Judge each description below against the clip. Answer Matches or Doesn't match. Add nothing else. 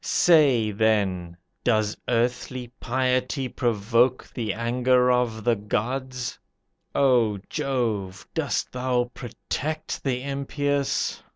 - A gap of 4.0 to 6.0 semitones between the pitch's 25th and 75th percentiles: Doesn't match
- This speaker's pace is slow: Matches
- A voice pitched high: Doesn't match